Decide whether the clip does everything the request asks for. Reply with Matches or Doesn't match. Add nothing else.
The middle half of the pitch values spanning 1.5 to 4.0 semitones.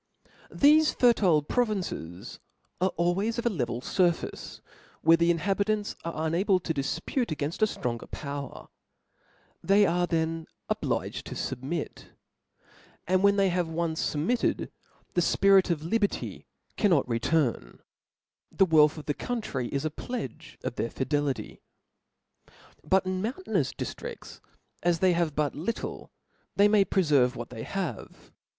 Doesn't match